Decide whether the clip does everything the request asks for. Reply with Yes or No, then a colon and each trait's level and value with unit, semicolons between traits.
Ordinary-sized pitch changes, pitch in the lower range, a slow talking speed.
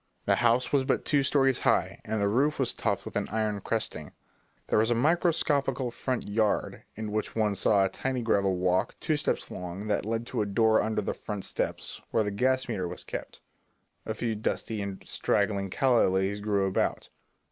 No: average, 4.0 semitones; low, 110 Hz; average, 195 wpm